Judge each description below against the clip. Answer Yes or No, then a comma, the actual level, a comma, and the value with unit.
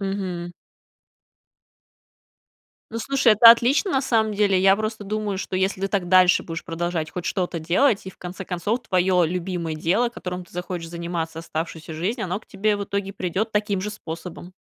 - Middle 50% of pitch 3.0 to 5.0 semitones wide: Yes, average, 3.3 semitones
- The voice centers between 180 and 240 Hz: Yes, high, 190 Hz